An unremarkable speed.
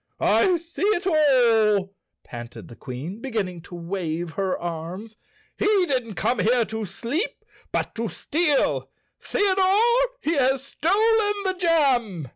No: slow, 130 wpm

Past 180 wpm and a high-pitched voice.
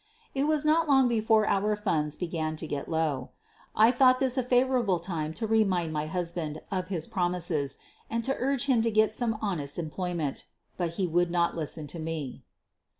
No: average, 190 wpm; medium, 180 Hz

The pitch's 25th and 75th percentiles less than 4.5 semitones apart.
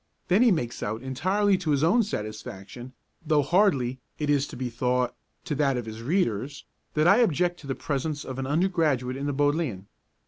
No: average, 5.3 semitones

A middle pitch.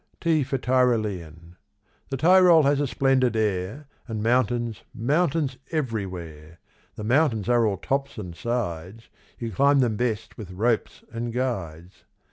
No: low, 120 Hz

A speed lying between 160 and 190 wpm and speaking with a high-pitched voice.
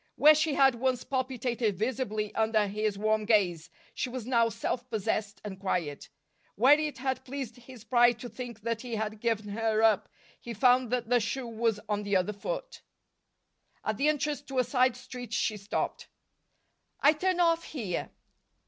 Yes: average, 175 wpm; high, 235 Hz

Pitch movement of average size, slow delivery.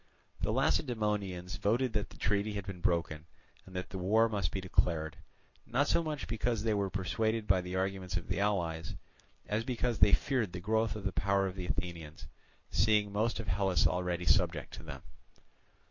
No: average, 3.2 semitones; average, 185 wpm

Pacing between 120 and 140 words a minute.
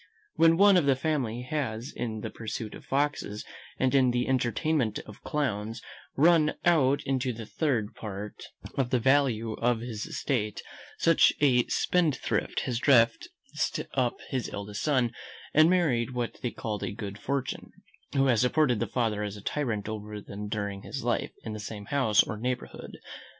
No: average, 165 wpm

